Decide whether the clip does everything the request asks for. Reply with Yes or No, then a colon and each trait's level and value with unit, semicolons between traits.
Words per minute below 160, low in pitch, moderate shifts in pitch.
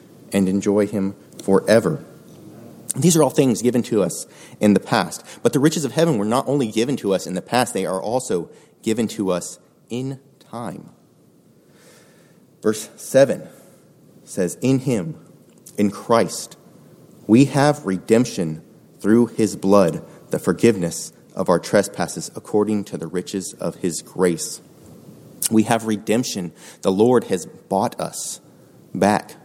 Yes: average, 145 wpm; low, 110 Hz; average, 4.1 semitones